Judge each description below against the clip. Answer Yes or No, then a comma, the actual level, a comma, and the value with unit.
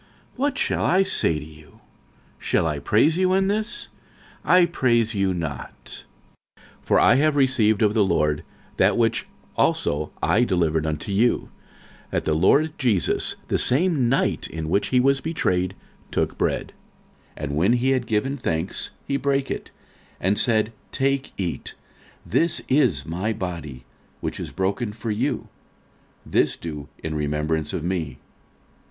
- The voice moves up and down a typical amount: No, wide, 8.9 semitones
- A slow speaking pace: No, average, 155 wpm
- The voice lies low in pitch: Yes, low, 105 Hz